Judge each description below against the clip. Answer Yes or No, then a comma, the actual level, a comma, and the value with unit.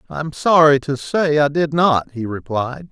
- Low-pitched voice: No, medium, 145 Hz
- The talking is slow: No, fast, 205 wpm